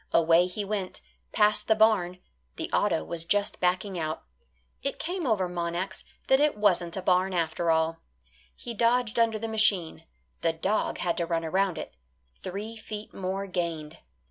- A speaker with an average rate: Yes, average, 165 wpm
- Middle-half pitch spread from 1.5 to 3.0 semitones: No, average, 4.1 semitones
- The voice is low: No, medium, 185 Hz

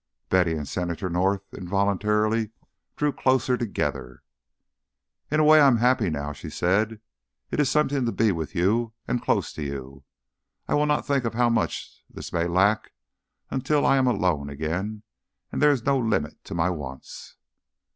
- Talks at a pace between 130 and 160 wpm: No, average, 170 wpm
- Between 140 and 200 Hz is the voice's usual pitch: No, low, 105 Hz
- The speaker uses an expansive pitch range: Yes, wide, 6.5 semitones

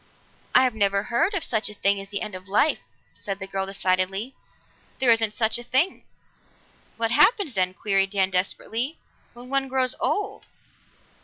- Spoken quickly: No, average, 165 wpm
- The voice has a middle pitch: No, high, 220 Hz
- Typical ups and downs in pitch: Yes, average, 4.8 semitones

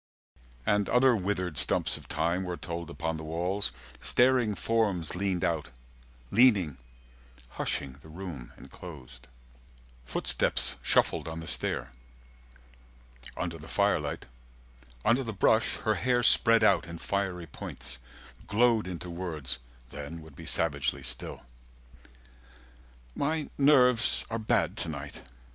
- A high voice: No, very low, 90 Hz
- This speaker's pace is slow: Yes, slow, 125 wpm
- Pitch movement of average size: No, wide, 5.8 semitones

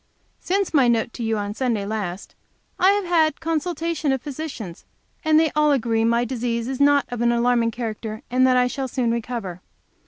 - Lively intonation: No, average, 4.5 semitones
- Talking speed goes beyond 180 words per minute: Yes, average, 200 wpm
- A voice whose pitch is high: Yes, high, 245 Hz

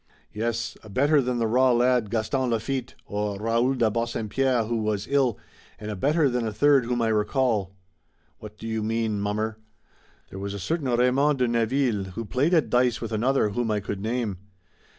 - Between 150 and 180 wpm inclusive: No, average, 190 wpm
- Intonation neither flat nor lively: Yes, average, 3.1 semitones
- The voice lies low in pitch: Yes, low, 115 Hz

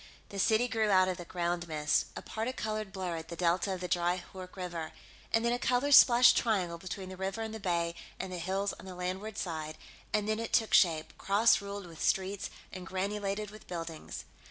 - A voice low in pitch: No, high, 190 Hz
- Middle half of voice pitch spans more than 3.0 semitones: Yes, average, 3.5 semitones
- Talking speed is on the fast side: Yes, fast, 210 wpm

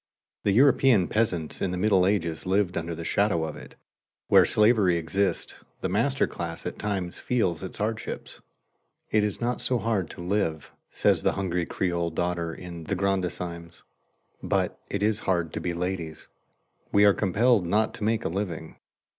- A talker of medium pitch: No, very low, 95 Hz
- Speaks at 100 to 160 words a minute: No, average, 170 wpm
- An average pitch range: Yes, average, 3.5 semitones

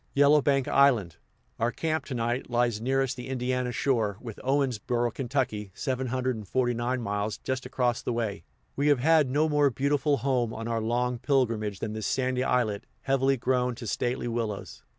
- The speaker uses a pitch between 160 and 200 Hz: No, low, 125 Hz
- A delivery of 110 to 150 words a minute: No, average, 160 wpm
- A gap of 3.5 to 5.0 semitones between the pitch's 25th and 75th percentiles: No, narrow, 2.6 semitones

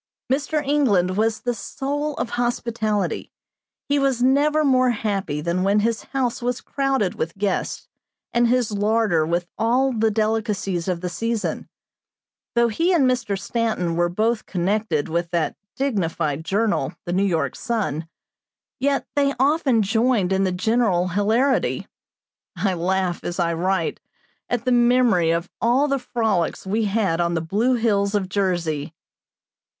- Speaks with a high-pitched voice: Yes, high, 215 Hz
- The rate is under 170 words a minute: Yes, average, 150 wpm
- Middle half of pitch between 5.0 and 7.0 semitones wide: Yes, wide, 5.4 semitones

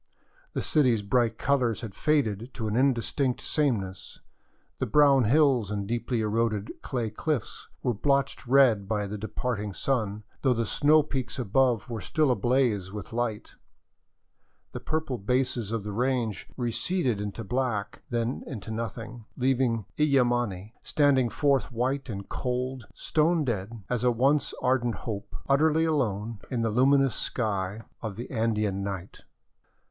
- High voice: No, low, 120 Hz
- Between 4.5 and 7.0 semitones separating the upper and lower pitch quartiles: No, average, 3.8 semitones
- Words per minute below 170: Yes, average, 140 wpm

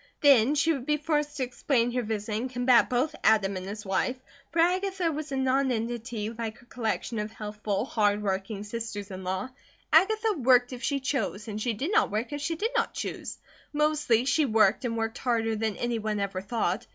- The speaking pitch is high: Yes, high, 235 Hz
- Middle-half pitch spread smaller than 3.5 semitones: No, average, 4.8 semitones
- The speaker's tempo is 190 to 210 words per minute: Yes, fast, 205 wpm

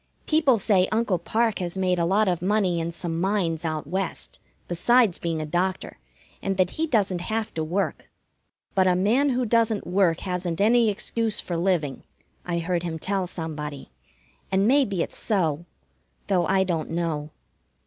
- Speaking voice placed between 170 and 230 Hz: Yes, medium, 185 Hz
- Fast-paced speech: No, average, 170 wpm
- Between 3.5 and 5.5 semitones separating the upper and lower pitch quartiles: Yes, average, 3.8 semitones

